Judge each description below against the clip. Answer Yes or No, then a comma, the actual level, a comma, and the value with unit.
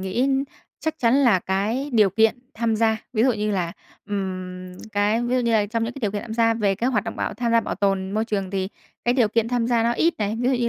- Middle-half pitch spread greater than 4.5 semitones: No, average, 3.0 semitones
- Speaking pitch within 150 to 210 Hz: No, high, 225 Hz